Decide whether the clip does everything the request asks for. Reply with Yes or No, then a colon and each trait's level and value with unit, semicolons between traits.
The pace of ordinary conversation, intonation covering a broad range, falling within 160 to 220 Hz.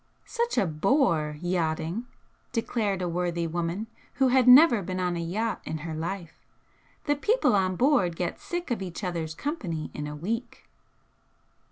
Yes: average, 160 wpm; wide, 6.3 semitones; medium, 185 Hz